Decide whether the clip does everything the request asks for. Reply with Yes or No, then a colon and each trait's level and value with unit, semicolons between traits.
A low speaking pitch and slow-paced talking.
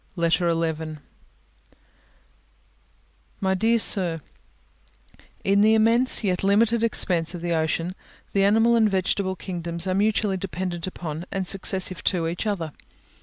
No: medium, 185 Hz; slow, 125 wpm